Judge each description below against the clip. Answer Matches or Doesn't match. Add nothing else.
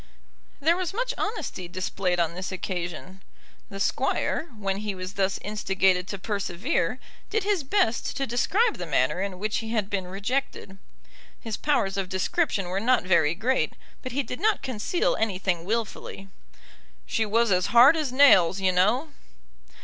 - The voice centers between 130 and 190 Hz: Doesn't match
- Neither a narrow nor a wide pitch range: Doesn't match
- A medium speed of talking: Matches